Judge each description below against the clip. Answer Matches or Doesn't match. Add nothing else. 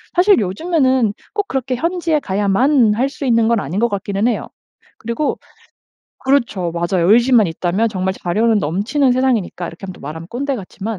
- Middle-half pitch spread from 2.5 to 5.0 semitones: Doesn't match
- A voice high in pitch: Matches